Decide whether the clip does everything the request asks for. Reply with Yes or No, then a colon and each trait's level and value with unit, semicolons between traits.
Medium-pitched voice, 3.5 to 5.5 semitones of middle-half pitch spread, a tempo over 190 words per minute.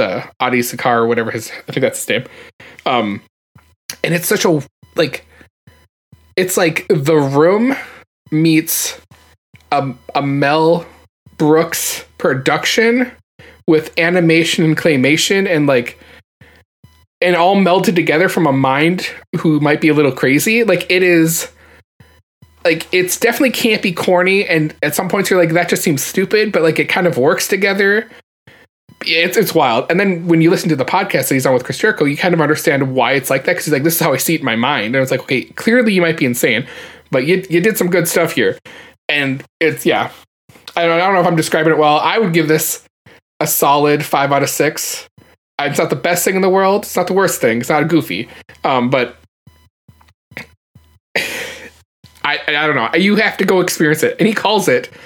Yes: medium, 165 Hz; average, 4.0 semitones; average, 200 wpm